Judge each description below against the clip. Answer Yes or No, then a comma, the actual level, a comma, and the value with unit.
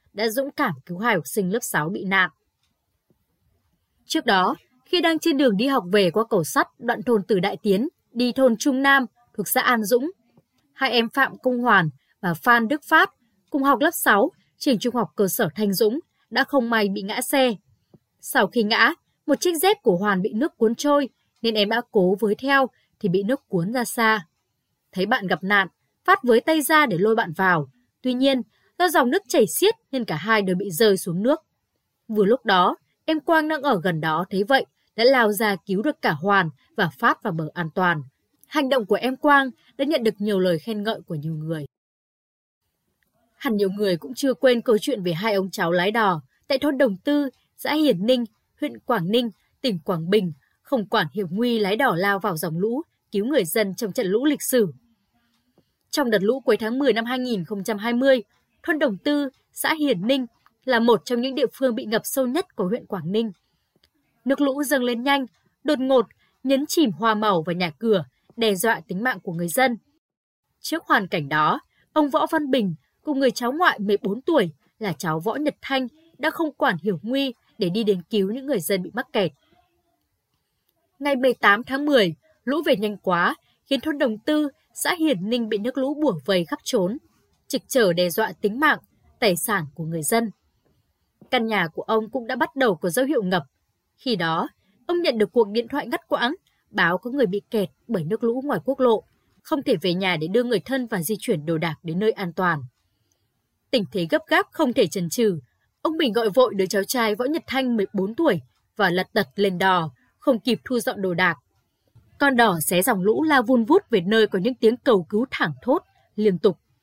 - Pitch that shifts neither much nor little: No, wide, 6.0 semitones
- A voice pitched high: Yes, high, 225 Hz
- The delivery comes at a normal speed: Yes, average, 210 wpm